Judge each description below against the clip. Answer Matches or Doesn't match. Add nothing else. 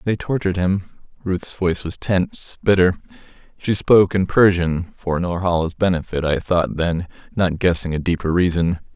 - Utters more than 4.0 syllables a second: Matches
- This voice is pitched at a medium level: Doesn't match